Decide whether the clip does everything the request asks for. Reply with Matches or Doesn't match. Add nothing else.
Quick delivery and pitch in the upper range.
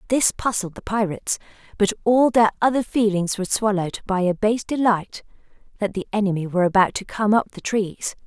Doesn't match